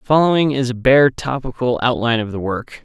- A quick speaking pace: No, average, 190 wpm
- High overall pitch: No, low, 125 Hz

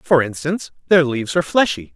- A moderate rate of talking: Yes, average, 185 wpm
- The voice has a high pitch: No, medium, 145 Hz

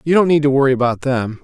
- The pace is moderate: No, fast, 295 wpm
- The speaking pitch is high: No, medium, 140 Hz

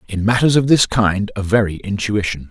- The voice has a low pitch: Yes, low, 105 Hz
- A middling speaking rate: Yes, average, 190 wpm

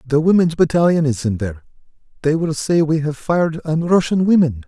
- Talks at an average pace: Yes, average, 180 wpm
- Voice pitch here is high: No, medium, 155 Hz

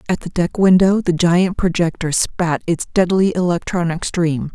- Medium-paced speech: Yes, average, 160 wpm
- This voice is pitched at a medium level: Yes, medium, 175 Hz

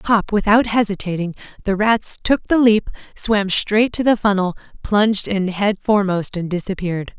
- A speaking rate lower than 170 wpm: Yes, average, 160 wpm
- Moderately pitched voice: No, high, 205 Hz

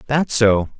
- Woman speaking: No, male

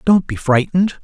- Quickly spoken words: No, average, 175 wpm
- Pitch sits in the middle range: Yes, medium, 160 Hz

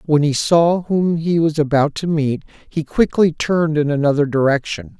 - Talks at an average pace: Yes, average, 180 wpm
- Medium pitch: Yes, medium, 155 Hz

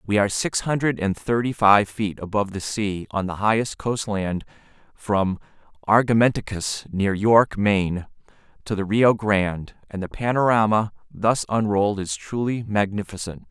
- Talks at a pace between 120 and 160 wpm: Yes, average, 140 wpm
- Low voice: Yes, low, 105 Hz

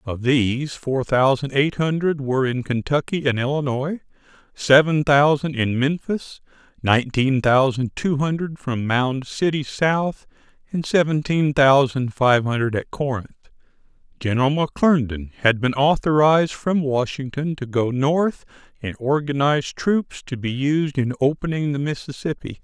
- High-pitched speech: No, medium, 140 Hz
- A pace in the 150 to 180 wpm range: No, slow, 135 wpm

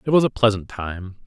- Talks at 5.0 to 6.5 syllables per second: Yes, 5.6 syllables/s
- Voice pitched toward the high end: No, low, 110 Hz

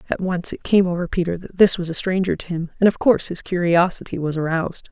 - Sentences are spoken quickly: Yes, fast, 245 wpm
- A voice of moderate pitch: Yes, medium, 175 Hz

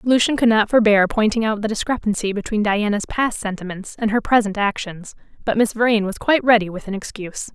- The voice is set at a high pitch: Yes, high, 215 Hz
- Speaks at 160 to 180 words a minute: No, average, 200 wpm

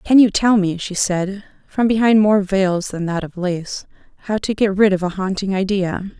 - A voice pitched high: Yes, high, 195 Hz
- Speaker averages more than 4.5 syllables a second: Yes, 4.7 syllables/s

